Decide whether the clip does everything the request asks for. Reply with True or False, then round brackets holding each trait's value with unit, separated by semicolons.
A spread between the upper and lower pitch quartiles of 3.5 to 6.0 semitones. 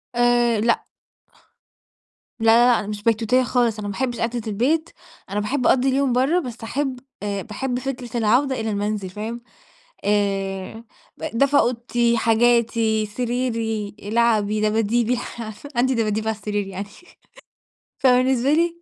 False (2.9 semitones)